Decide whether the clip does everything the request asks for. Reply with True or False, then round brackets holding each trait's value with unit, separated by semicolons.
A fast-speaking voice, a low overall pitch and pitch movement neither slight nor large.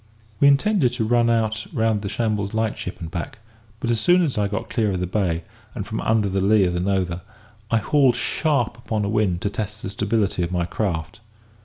True (220 wpm; 105 Hz; 3.3 semitones)